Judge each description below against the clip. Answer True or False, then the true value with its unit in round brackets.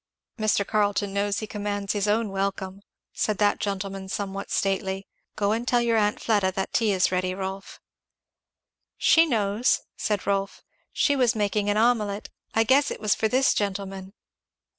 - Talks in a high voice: True (205 Hz)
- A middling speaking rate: True (160 wpm)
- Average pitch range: False (1.8 semitones)